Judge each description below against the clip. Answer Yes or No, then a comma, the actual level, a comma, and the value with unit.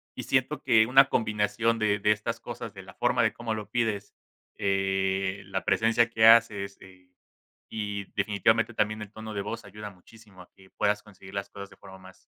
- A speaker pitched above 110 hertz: No, low, 105 Hz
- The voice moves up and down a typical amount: No, narrow, 2.2 semitones